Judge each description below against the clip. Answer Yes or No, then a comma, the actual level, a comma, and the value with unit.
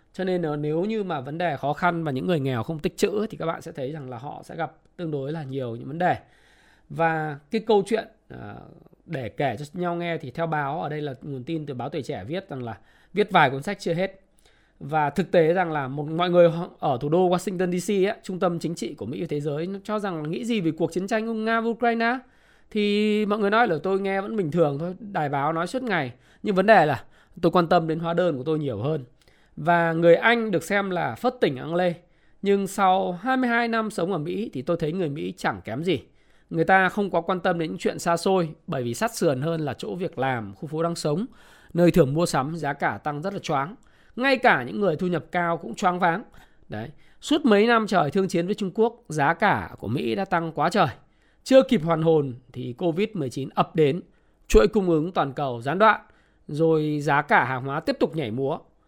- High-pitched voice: No, medium, 170 Hz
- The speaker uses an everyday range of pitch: Yes, average, 4.5 semitones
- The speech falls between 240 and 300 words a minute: Yes, average, 245 wpm